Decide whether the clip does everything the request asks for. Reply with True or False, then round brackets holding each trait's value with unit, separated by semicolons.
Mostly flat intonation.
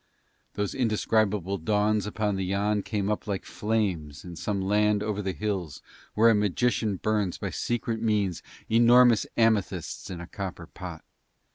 True (2.1 semitones)